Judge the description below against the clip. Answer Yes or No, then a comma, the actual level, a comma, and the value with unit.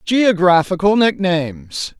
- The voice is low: No, medium, 185 Hz